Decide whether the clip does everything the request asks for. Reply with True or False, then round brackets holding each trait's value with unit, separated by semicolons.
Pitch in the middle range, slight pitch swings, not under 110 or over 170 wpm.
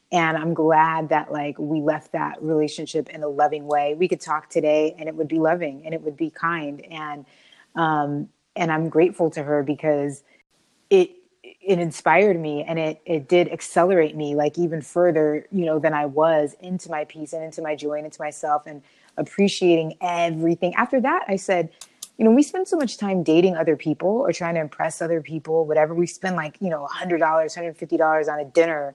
False (160 Hz; 2.3 semitones; 200 wpm)